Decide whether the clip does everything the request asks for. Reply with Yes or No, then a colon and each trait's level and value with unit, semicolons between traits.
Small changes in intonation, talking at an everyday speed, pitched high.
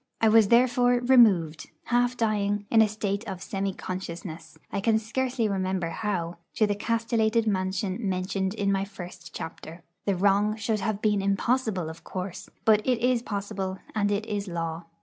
No: average, 3.0 semitones; average, 170 wpm; high, 205 Hz